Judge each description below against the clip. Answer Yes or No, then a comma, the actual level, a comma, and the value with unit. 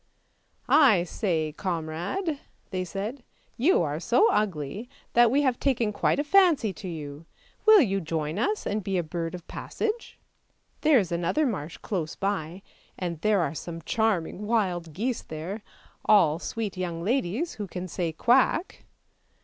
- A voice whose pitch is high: Yes, high, 195 Hz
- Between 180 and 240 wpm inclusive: No, average, 160 wpm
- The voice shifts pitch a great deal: Yes, wide, 6.2 semitones